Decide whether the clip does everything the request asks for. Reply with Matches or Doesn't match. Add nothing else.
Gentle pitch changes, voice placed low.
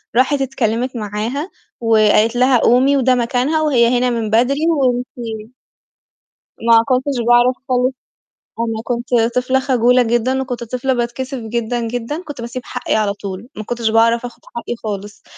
Doesn't match